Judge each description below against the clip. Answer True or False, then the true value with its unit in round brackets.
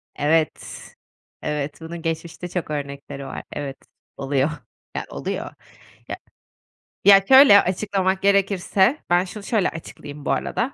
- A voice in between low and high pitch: True (175 Hz)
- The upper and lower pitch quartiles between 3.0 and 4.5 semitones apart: False (5.1 semitones)